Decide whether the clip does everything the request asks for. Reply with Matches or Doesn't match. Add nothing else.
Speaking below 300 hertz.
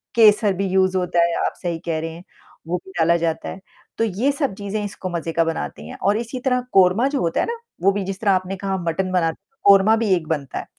Matches